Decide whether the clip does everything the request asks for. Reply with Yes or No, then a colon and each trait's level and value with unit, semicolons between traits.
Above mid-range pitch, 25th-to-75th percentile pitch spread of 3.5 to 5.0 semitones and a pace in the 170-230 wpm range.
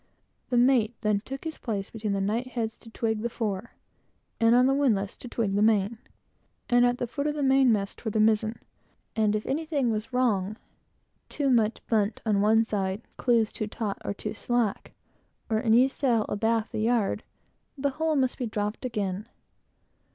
No: high, 225 Hz; average, 2.8 semitones; average, 175 wpm